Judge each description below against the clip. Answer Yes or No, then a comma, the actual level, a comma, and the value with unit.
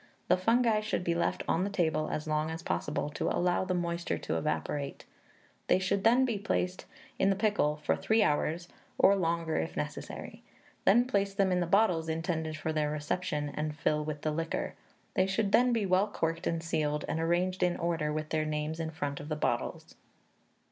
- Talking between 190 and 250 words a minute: Yes, average, 195 wpm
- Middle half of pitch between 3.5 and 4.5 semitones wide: Yes, average, 3.8 semitones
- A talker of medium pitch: Yes, medium, 170 Hz